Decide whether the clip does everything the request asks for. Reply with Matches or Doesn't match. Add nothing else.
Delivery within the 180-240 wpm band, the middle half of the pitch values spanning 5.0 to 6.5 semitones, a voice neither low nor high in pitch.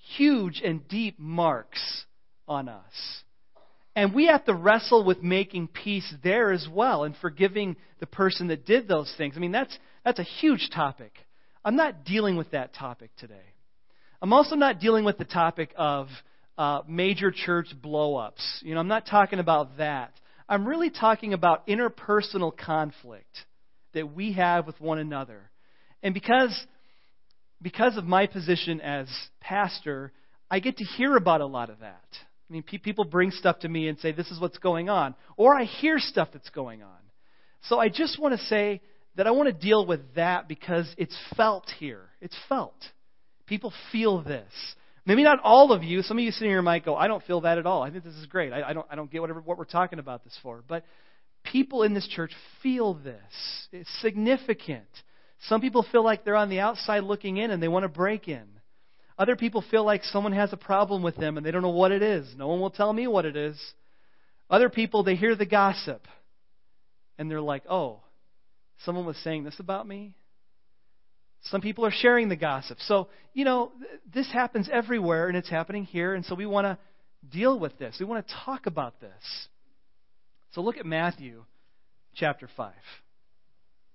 Matches